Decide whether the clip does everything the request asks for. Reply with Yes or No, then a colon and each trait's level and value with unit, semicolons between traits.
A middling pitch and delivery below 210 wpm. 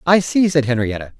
Yes: medium, 145 Hz; average, 200 wpm